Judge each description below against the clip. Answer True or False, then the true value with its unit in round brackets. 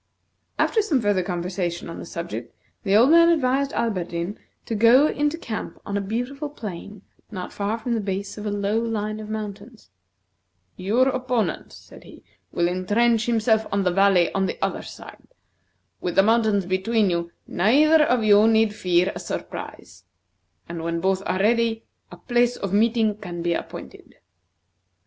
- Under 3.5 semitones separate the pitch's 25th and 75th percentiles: False (4.0 semitones)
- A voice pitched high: True (210 Hz)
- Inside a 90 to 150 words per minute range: False (165 wpm)